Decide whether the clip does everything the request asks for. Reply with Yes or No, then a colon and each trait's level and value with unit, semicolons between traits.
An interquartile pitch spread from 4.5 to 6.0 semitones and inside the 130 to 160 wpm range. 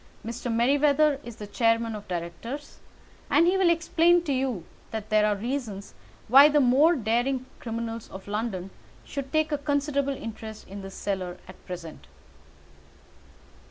Yes: average, 5.3 semitones; average, 150 wpm